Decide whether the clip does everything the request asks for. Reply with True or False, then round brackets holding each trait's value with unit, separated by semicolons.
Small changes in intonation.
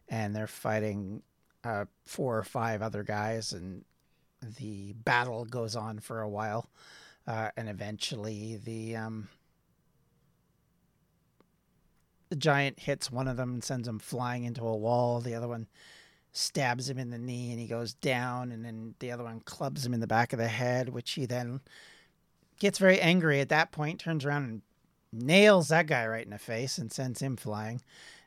False (3.2 semitones)